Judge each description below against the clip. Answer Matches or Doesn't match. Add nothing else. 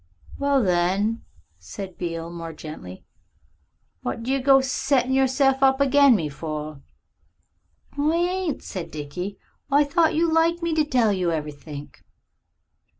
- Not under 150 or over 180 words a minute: Doesn't match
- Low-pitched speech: Doesn't match